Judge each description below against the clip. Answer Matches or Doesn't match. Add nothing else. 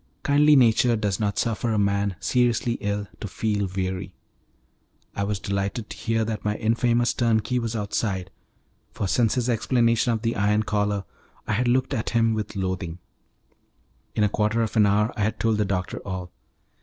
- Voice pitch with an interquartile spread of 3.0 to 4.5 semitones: Doesn't match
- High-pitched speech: Doesn't match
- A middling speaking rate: Matches